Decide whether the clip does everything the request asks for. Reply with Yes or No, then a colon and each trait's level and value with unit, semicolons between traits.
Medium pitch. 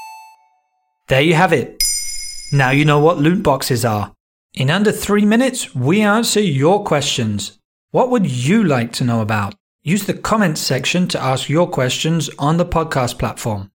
Yes: medium, 150 Hz